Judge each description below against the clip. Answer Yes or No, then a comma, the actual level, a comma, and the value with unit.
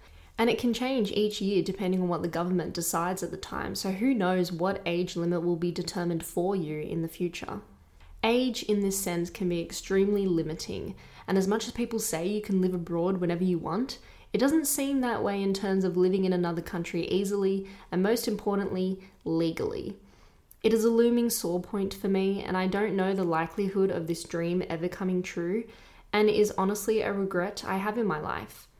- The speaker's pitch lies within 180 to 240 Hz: Yes, high, 190 Hz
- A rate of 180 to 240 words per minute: Yes, fast, 205 wpm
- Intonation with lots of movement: No, average, 3.0 semitones